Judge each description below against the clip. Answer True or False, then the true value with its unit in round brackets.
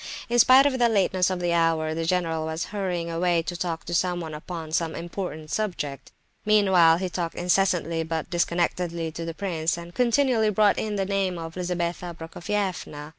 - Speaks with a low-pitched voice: False (175 Hz)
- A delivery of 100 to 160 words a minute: False (175 wpm)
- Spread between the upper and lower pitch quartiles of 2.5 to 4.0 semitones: True (2.8 semitones)